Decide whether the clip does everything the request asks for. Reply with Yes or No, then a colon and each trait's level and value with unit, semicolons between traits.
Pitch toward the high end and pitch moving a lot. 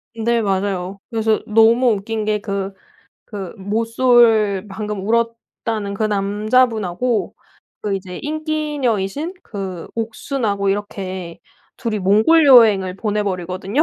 No: high, 210 Hz; average, 2.9 semitones